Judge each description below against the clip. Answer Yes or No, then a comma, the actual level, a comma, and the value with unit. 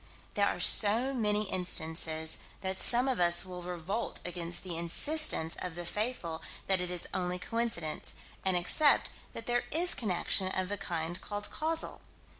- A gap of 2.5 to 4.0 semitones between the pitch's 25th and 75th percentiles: No, average, 4.8 semitones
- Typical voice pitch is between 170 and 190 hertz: Yes, medium, 185 Hz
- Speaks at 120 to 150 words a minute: No, average, 160 wpm